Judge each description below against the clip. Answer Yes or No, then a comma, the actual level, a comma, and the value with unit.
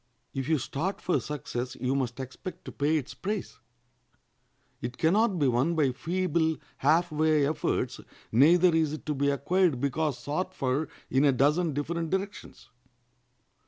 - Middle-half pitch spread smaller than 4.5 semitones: Yes, average, 3.9 semitones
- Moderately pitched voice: Yes, medium, 155 Hz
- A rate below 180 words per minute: Yes, average, 160 wpm